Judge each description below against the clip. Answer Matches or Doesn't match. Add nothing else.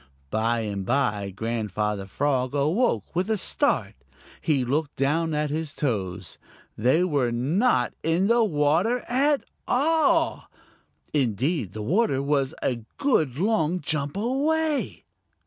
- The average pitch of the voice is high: Doesn't match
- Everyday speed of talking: Doesn't match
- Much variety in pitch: Matches